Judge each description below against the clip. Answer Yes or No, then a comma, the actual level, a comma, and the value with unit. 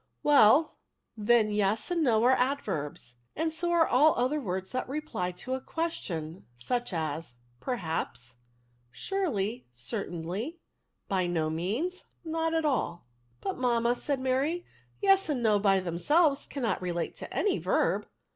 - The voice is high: Yes, high, 240 Hz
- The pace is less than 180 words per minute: Yes, average, 155 wpm